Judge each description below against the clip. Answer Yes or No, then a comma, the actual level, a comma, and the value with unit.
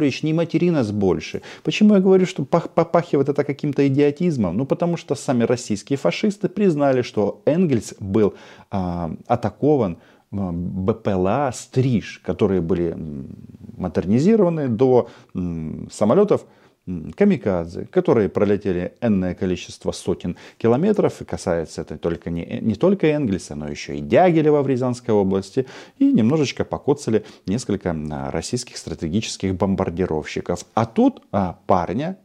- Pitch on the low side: Yes, low, 115 Hz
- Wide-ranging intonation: Yes, wide, 8.9 semitones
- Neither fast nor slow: Yes, average, 125 wpm